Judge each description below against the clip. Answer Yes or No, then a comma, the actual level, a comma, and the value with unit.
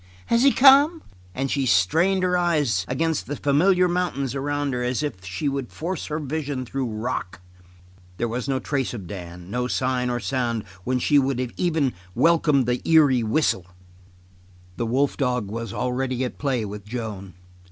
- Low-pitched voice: Yes, low, 130 Hz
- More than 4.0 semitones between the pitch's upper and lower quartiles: Yes, average, 4.4 semitones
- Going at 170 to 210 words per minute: Yes, average, 175 wpm